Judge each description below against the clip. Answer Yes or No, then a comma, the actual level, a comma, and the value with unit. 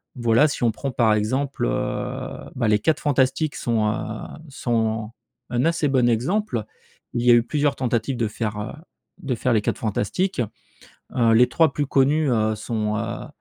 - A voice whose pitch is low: Yes, low, 120 Hz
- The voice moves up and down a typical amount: Yes, average, 3.7 semitones